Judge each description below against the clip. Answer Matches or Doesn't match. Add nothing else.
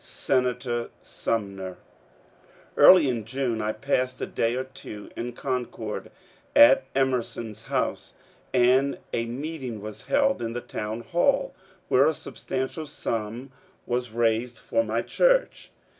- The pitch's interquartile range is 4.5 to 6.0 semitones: Doesn't match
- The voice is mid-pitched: Doesn't match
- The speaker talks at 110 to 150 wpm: Matches